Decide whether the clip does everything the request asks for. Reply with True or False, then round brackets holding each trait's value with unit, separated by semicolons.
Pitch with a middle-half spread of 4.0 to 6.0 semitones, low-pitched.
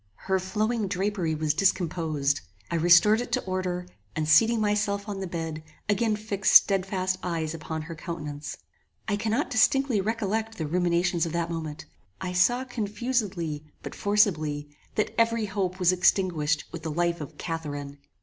False (4.4 semitones; 185 Hz)